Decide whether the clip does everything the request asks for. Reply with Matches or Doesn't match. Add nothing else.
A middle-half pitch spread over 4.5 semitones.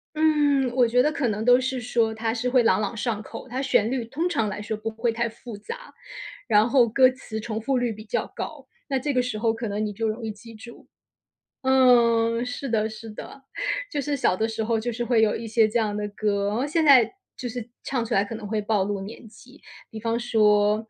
Doesn't match